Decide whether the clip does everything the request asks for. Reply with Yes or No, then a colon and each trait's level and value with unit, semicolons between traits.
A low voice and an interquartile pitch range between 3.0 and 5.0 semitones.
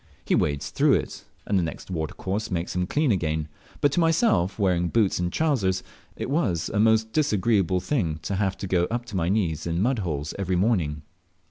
Yes: very low, 95 Hz; average, 4.6 semitones